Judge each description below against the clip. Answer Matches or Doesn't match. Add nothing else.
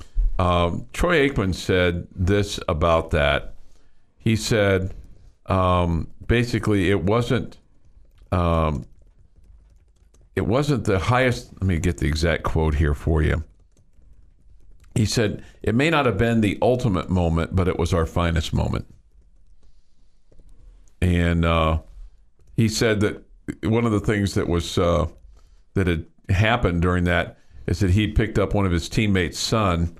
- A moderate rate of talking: Matches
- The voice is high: Doesn't match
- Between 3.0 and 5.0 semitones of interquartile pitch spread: Matches